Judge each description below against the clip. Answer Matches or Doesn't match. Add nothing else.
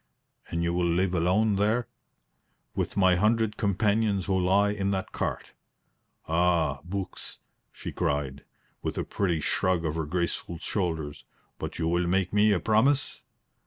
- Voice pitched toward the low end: Matches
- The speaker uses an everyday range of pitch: Matches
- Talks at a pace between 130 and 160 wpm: Matches